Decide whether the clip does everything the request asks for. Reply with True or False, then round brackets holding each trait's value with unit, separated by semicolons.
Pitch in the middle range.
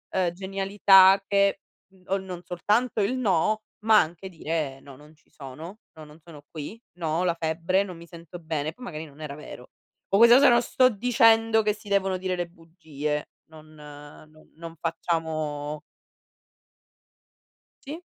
True (170 Hz)